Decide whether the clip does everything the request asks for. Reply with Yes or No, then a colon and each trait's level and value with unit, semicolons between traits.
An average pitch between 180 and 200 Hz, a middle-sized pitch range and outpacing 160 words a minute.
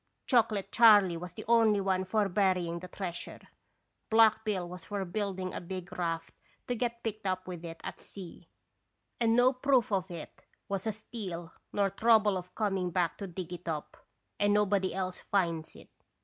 Yes: high, 190 Hz; average, 3.3 semitones; average, 175 wpm